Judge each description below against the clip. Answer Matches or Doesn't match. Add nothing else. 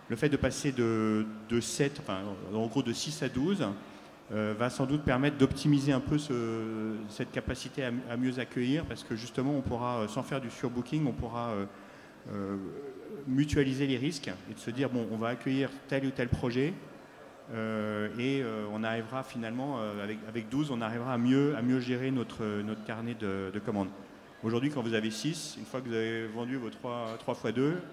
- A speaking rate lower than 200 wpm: Doesn't match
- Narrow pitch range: Doesn't match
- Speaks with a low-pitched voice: Matches